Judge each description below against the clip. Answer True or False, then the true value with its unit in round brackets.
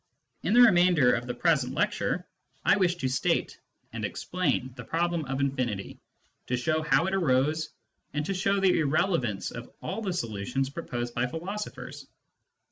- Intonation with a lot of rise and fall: True (6.2 semitones)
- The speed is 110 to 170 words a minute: True (160 wpm)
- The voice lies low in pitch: False (155 Hz)